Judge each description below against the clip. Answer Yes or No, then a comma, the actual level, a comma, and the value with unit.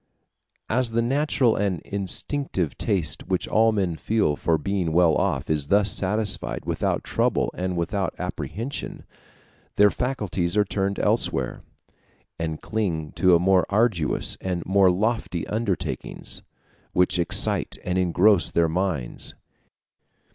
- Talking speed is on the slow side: Yes, slow, 125 wpm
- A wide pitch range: No, average, 3.7 semitones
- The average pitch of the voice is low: Yes, very low, 95 Hz